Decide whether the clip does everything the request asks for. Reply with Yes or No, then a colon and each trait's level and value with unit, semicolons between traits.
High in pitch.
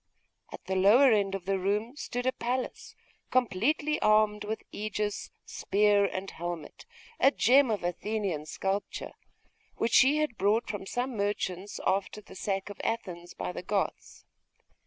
Yes: high, 210 Hz